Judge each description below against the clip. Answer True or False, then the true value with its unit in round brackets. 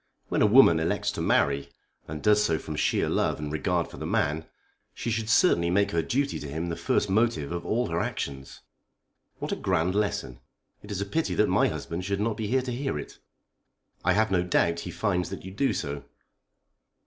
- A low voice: True (90 Hz)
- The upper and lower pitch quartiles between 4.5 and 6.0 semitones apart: True (5.0 semitones)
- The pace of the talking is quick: True (210 wpm)